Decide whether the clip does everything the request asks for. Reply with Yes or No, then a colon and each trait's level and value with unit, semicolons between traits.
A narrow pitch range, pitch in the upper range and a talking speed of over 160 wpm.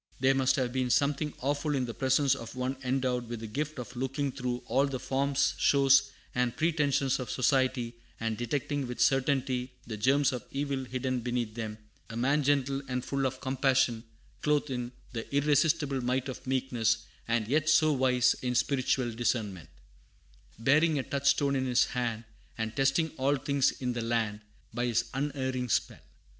No: narrow, 2.3 semitones; low, 130 Hz; average, 170 wpm